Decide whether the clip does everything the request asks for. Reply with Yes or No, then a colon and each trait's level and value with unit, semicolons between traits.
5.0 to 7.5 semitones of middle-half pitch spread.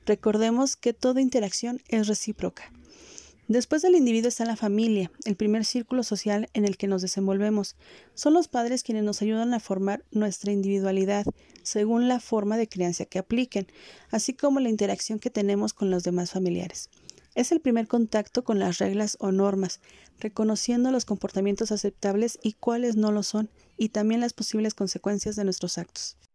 No: average, 3.0 semitones